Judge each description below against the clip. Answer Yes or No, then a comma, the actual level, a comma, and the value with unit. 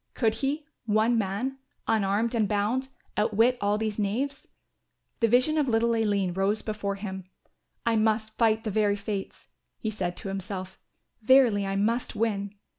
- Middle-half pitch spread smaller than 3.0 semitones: Yes, narrow, 2.5 semitones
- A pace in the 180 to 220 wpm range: No, average, 155 wpm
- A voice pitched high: Yes, high, 215 Hz